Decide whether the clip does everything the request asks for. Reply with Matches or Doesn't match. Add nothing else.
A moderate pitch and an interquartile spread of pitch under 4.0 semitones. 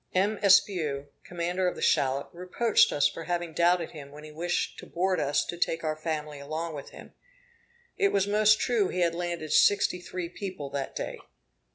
Matches